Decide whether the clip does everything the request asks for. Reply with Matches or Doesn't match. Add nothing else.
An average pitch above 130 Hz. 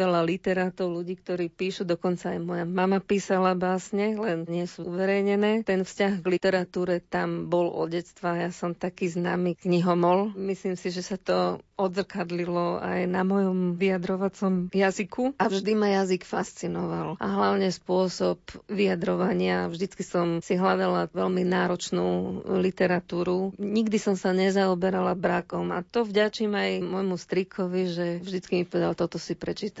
Matches